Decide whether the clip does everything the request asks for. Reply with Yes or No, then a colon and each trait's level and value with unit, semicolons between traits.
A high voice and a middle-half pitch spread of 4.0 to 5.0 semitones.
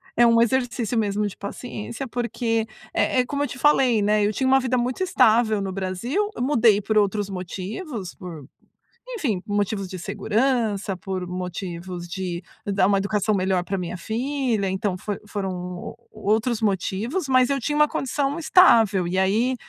Yes: high, 210 Hz; average, 4.6 semitones